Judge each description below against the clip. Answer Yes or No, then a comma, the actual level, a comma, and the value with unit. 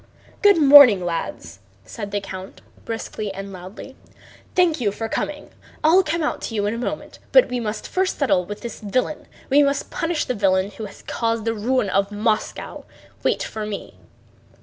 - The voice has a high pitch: Yes, high, 225 Hz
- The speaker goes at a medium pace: Yes, average, 180 wpm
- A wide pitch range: Yes, wide, 5.9 semitones